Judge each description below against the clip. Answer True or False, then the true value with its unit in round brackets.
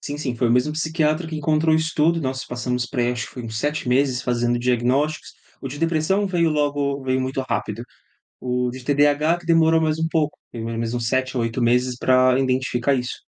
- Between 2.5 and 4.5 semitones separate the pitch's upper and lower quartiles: True (3.9 semitones)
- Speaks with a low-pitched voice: True (130 Hz)